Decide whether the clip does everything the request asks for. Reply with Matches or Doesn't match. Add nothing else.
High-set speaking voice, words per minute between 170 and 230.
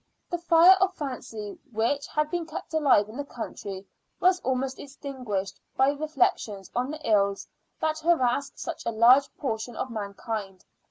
Doesn't match